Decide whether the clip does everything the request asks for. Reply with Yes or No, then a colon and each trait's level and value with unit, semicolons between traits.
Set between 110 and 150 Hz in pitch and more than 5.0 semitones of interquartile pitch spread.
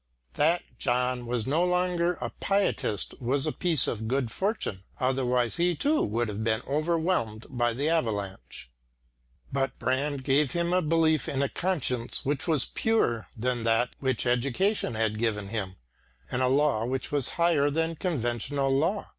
Yes: low, 135 Hz; wide, 5.5 semitones